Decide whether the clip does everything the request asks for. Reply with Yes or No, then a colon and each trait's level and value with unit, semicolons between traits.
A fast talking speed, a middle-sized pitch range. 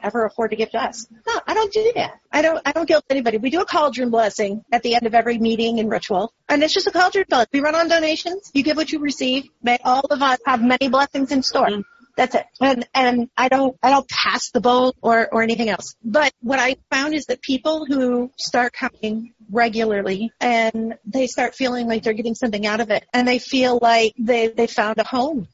Yes: fast, 235 wpm; average, 3.5 semitones